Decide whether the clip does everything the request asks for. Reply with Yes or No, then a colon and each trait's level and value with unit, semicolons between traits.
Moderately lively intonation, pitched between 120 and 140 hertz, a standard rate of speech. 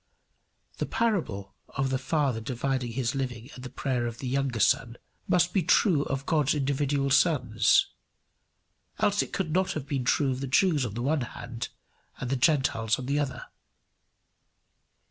Yes: average, 3.1 semitones; low, 135 Hz; average, 165 wpm